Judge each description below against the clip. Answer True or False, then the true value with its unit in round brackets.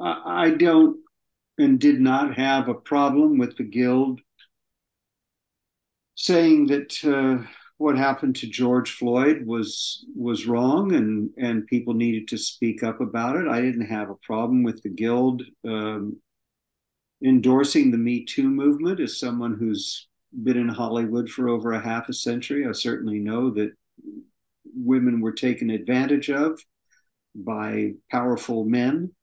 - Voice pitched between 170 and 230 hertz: False (125 Hz)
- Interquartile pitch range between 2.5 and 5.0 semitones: False (5.5 semitones)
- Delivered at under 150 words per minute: True (140 wpm)